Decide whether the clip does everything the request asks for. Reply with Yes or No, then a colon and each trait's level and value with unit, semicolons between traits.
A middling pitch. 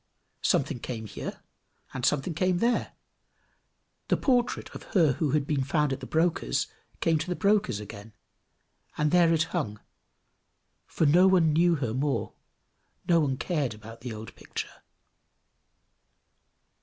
Yes: medium, 150 Hz